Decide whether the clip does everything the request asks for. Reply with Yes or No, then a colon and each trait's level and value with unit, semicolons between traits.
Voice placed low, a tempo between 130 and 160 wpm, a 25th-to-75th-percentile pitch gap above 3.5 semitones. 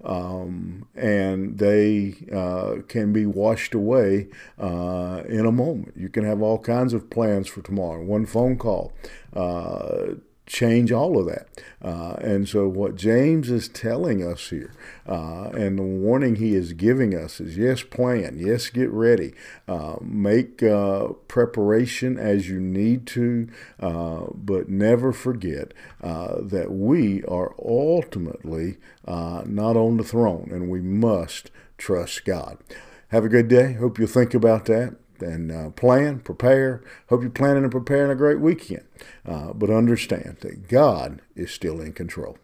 Yes: low, 105 Hz; average, 155 wpm; average, 4.2 semitones